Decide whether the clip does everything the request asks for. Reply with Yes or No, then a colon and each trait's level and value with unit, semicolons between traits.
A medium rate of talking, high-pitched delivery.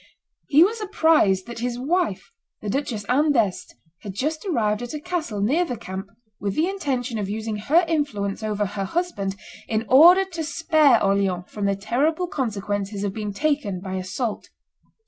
Yes: average, 170 wpm; high, 235 Hz